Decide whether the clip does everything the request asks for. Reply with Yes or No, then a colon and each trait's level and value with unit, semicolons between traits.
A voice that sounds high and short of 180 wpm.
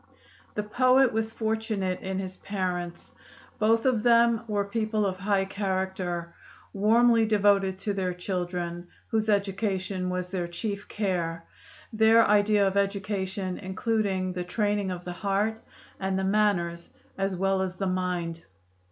Yes: high, 195 Hz; average, 140 wpm